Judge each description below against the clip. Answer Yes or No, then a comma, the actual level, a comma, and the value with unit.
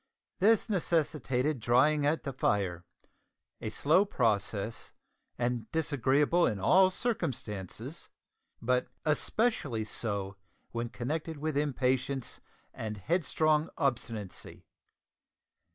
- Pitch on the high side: No, low, 135 Hz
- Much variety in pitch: Yes, wide, 5.7 semitones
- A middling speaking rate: No, slow, 90 wpm